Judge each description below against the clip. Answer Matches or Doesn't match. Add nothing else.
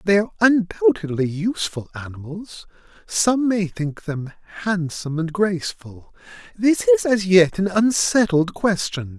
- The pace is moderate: Doesn't match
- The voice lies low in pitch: Doesn't match